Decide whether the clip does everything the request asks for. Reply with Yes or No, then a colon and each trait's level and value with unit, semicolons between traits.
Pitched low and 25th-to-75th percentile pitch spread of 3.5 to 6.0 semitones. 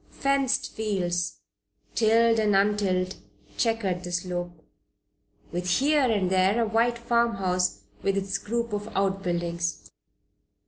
No: high, 195 Hz; average, 4.0 semitones